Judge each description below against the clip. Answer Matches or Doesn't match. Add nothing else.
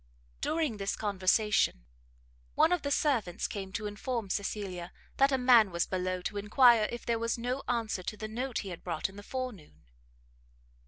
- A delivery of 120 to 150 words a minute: Doesn't match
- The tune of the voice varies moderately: Matches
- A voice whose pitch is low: Doesn't match